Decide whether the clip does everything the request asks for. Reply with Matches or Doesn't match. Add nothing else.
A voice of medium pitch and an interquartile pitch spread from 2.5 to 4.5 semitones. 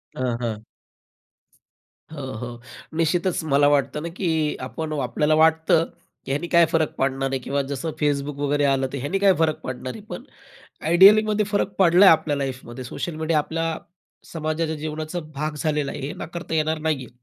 Matches